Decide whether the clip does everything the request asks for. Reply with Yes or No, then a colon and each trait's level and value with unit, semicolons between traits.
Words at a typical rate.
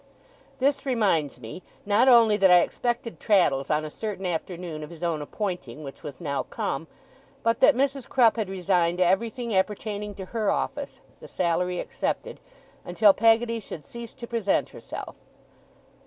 Yes: average, 155 wpm